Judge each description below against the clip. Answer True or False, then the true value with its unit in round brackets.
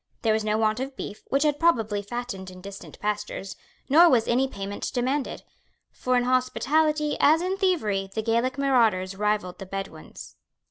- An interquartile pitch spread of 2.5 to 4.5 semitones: False (5.2 semitones)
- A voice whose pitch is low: False (235 Hz)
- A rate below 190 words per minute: True (170 wpm)